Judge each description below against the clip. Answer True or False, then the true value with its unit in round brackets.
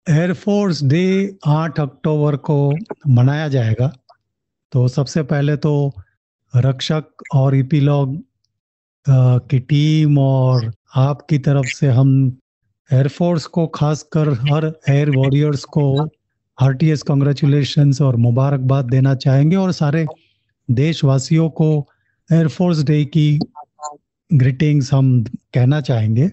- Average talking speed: False (105 wpm)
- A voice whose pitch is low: False (145 Hz)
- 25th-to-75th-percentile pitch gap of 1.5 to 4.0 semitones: True (2.8 semitones)